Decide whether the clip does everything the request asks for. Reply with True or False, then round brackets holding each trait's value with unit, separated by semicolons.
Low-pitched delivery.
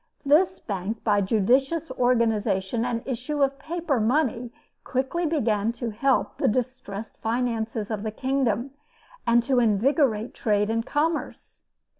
False (240 Hz)